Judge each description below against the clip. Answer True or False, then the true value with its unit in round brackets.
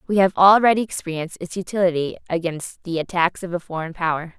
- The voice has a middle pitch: True (175 Hz)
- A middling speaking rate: True (180 wpm)